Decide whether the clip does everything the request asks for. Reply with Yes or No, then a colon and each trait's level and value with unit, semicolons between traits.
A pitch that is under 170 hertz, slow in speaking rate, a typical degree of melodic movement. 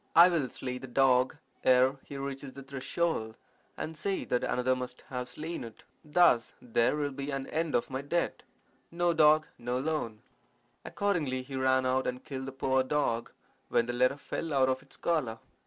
No: low, 135 Hz; average, 185 wpm; average, 3.0 semitones